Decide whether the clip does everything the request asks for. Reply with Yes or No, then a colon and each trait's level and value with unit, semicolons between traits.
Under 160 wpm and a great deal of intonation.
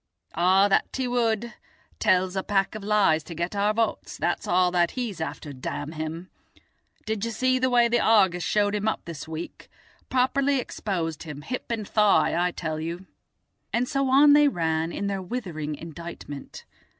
No: average, 175 wpm; wide, 5.7 semitones